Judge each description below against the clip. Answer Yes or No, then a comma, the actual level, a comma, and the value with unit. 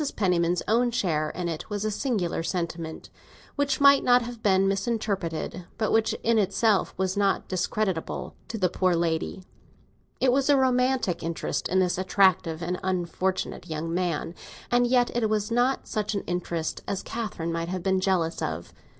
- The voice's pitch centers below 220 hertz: Yes, high, 190 Hz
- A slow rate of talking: No, average, 165 wpm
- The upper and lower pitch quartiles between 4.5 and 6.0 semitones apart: Yes, average, 4.8 semitones